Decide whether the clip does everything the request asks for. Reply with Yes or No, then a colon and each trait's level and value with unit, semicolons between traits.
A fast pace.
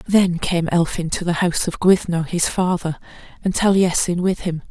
No: average, 180 wpm